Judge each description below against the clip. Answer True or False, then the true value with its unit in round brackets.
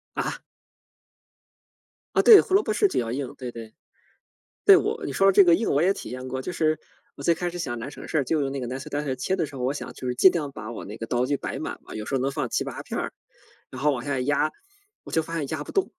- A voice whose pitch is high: False (145 Hz)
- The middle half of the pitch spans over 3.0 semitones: True (5.1 semitones)